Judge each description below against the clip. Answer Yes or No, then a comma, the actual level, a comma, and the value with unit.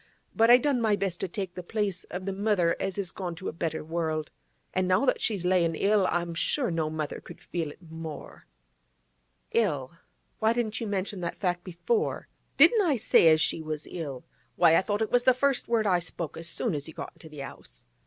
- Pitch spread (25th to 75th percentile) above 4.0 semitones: Yes, average, 4.6 semitones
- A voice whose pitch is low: No, medium, 180 Hz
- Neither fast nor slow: No, fast, 215 wpm